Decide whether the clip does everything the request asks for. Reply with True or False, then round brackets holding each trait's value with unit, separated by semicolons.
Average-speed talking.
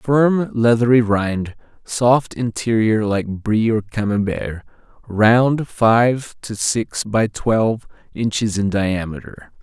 False (110 wpm)